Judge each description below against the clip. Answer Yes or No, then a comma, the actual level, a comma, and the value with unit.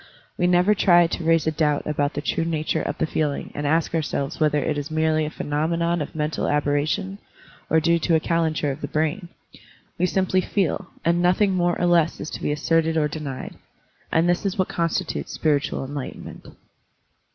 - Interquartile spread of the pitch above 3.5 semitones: No, narrow, 2.5 semitones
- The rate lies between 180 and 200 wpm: Yes, average, 190 wpm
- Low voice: No, medium, 160 Hz